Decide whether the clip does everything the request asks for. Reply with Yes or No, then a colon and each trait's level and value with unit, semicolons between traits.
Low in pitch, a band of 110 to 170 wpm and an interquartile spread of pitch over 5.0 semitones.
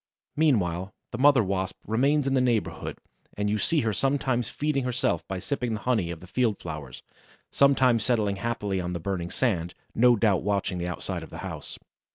No: low, 110 Hz; average, 190 wpm; wide, 5.4 semitones